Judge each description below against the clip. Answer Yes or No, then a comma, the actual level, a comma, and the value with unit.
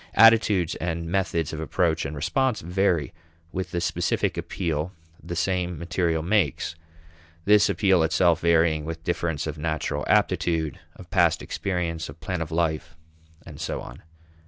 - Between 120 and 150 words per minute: Yes, average, 145 wpm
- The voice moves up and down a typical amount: No, narrow, 2.3 semitones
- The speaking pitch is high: No, very low, 85 Hz